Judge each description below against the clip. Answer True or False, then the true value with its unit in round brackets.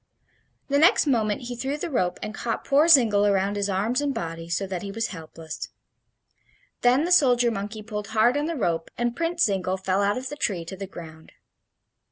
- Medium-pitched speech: False (215 Hz)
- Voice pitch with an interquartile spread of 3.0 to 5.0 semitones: False (5.4 semitones)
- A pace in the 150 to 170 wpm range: False (205 wpm)